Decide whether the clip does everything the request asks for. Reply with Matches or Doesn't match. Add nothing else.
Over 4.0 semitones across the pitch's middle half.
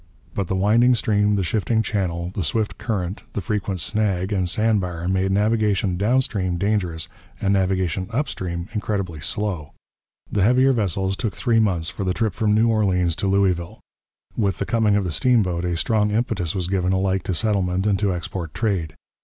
Doesn't match